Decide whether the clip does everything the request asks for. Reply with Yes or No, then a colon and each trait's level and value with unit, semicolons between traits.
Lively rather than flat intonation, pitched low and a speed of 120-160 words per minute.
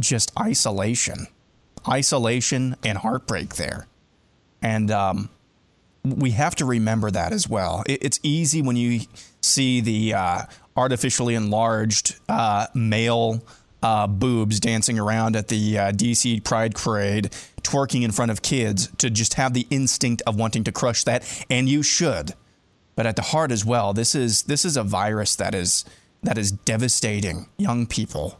No: average, 2.9 semitones; low, 115 Hz; average, 155 wpm